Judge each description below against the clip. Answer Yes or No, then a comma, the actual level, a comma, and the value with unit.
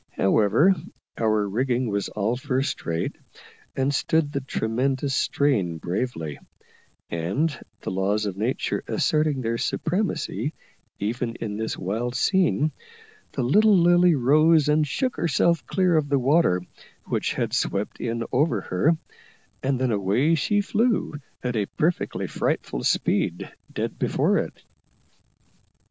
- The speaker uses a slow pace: Yes, slow, 130 wpm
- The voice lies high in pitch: No, low, 130 Hz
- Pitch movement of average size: No, wide, 6.5 semitones